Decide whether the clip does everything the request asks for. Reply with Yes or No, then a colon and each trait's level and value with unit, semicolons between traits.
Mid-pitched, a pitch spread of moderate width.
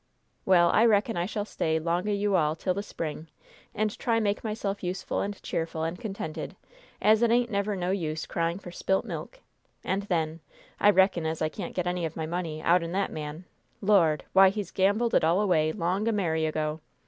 Yes: medium, 180 Hz; average, 3.9 semitones